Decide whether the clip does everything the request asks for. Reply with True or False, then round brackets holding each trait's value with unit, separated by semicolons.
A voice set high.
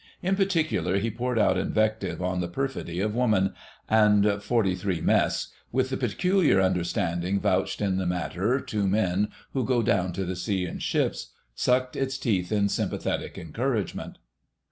False (105 Hz)